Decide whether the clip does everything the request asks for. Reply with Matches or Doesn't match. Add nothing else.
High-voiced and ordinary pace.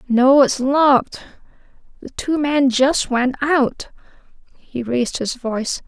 Doesn't match